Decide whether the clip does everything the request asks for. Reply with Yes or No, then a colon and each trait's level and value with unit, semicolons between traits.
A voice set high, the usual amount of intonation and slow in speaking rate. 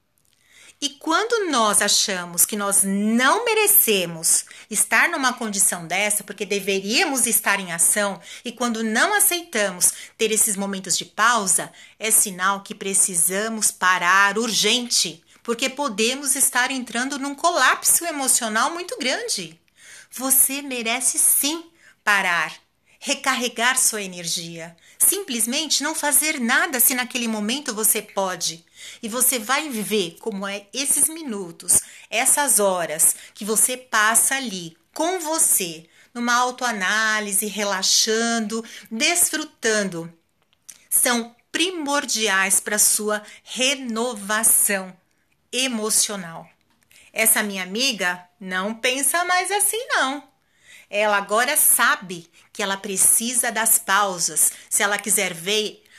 Yes: high, 220 Hz; average, 4.8 semitones; slow, 110 wpm